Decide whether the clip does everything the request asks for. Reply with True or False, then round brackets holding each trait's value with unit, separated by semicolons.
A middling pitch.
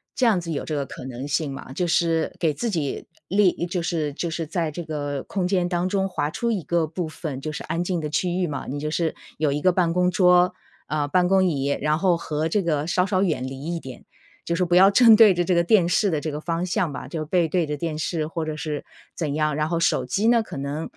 True (165 Hz)